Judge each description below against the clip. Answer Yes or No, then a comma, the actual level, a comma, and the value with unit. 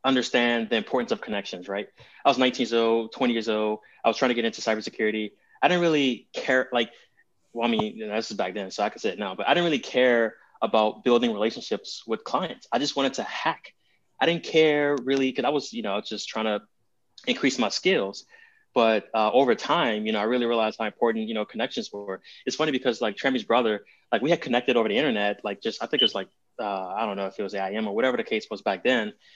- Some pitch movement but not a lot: Yes, average, 3.9 semitones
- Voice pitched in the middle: No, low, 115 Hz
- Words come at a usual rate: No, fast, 245 wpm